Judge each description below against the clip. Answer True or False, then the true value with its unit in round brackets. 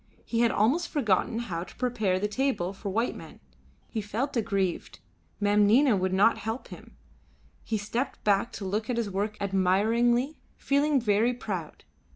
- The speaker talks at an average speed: True (165 wpm)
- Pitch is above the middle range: True (215 Hz)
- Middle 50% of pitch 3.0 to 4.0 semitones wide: True (3.4 semitones)